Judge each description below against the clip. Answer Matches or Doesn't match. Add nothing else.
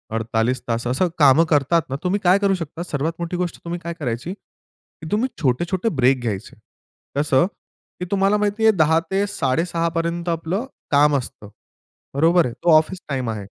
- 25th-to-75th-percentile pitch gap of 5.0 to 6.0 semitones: Matches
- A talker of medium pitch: Matches